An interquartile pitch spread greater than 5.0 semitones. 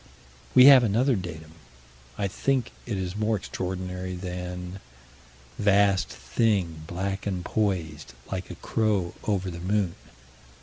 No: average, 2.7 semitones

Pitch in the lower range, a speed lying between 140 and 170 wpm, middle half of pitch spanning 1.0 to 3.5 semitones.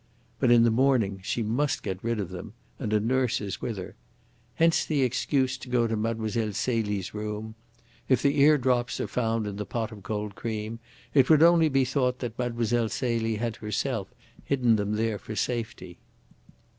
No: low, 115 Hz; average, 180 wpm; average, 3.1 semitones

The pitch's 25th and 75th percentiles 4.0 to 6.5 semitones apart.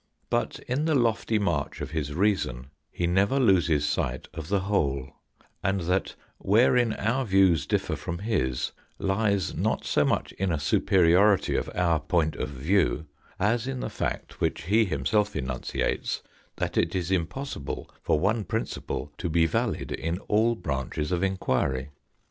Yes: wide, 5.4 semitones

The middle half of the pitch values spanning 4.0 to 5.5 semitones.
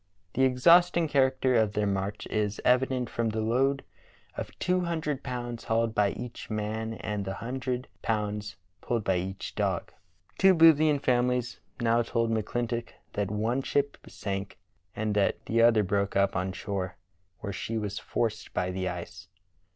No: average, 3.6 semitones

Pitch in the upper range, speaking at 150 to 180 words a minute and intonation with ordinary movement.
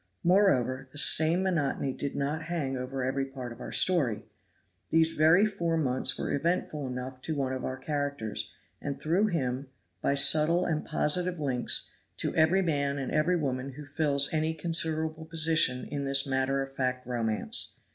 No: medium, 145 Hz; average, 165 wpm; average, 3.5 semitones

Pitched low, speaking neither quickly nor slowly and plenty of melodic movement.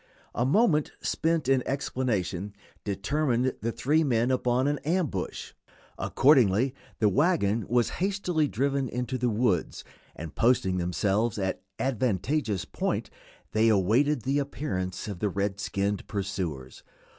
No: low, 120 Hz; slow, 130 wpm; wide, 5.7 semitones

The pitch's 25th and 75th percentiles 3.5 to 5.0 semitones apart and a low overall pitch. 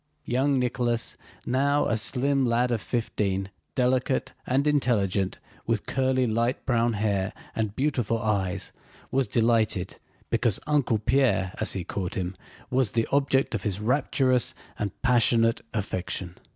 Yes: average, 4.0 semitones; low, 115 Hz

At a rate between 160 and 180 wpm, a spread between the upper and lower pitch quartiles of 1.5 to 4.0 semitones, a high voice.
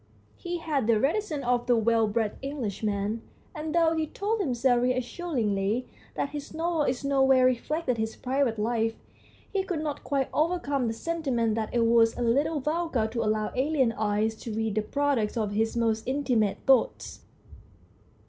No: average, 165 wpm; average, 5.0 semitones; very high, 250 Hz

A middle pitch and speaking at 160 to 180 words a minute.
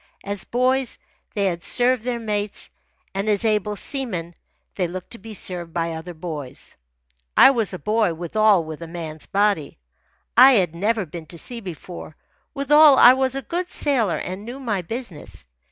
No: high, 205 Hz; average, 170 wpm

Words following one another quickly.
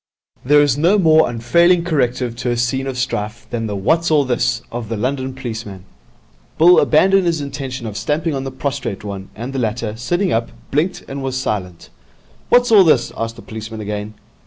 No: average, 190 wpm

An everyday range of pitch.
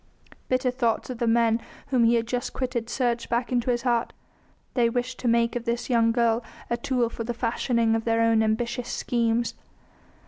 No: narrow, 1.1 semitones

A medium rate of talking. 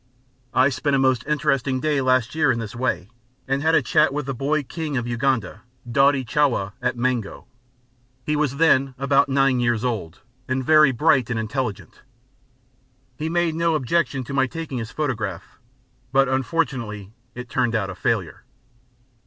Yes: average, 165 wpm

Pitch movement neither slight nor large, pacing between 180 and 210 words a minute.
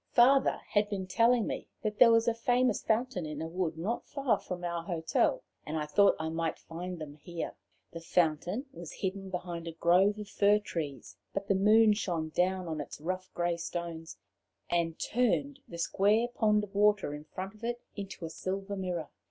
Yes: average, 4.1 semitones; average, 195 wpm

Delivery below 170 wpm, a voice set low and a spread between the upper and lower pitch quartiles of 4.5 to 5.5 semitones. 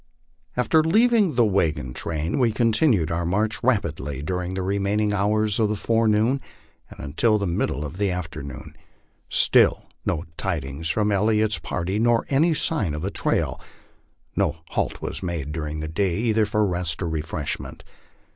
Yes: average, 160 wpm; low, 100 Hz; average, 5.2 semitones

